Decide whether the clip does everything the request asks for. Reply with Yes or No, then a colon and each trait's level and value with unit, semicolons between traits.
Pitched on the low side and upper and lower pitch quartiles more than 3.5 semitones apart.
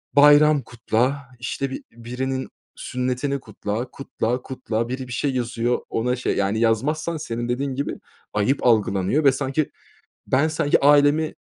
No: low, 130 Hz; average, 3.2 semitones